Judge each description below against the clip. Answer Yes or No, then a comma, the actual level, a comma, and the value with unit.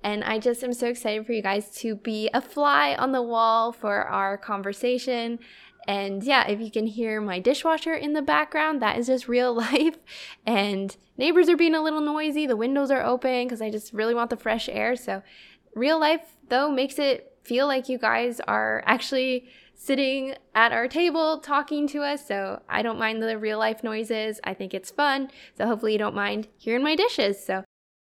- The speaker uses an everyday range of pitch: Yes, average, 4.6 semitones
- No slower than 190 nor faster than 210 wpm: Yes, average, 200 wpm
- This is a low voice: No, high, 240 Hz